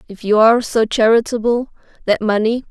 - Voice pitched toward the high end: Yes, high, 225 Hz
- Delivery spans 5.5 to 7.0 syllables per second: Yes, 5.6 syllables/s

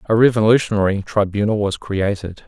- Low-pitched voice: Yes, low, 105 Hz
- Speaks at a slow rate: Yes, slow, 120 wpm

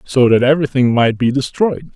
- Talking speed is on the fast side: No, average, 185 wpm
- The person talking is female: No, male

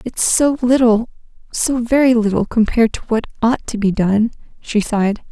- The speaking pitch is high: Yes, high, 230 Hz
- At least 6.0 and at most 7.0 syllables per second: No, 5.1 syllables/s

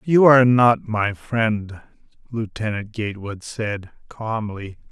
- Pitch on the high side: No, low, 110 Hz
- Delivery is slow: Yes, slow, 110 wpm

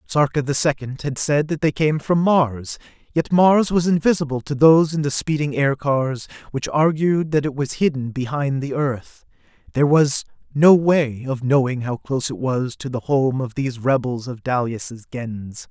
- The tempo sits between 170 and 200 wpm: Yes, average, 185 wpm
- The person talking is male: Yes, male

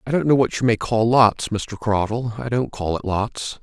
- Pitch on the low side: Yes, low, 115 Hz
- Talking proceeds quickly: Yes, fast, 250 wpm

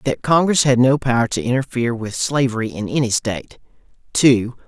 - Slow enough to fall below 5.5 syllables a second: No, 5.6 syllables/s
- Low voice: Yes, low, 125 Hz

